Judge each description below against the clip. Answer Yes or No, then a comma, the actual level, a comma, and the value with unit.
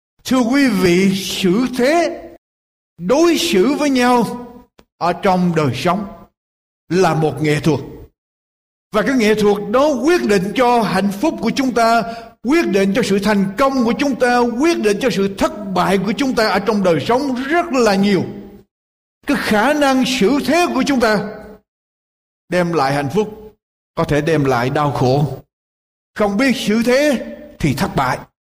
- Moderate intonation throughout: No, wide, 6.2 semitones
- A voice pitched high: Yes, high, 215 Hz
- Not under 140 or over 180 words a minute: Yes, average, 170 wpm